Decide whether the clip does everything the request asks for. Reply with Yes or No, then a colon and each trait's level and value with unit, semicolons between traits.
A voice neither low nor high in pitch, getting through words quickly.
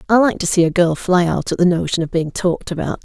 Yes: medium, 175 Hz; fast, 295 wpm